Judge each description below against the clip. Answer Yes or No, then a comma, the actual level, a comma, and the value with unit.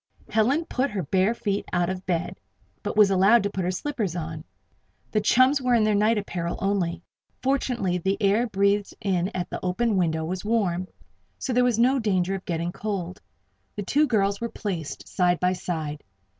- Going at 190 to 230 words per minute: Yes, average, 195 wpm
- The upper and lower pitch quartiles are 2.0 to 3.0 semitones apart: No, average, 3.9 semitones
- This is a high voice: Yes, high, 195 Hz